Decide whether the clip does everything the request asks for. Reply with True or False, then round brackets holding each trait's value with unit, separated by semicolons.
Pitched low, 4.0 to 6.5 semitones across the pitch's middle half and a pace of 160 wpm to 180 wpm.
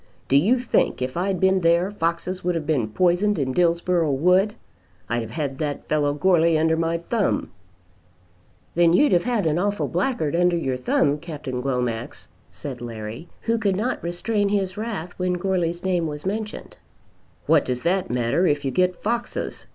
False (170 Hz; 4.5 semitones; 175 wpm)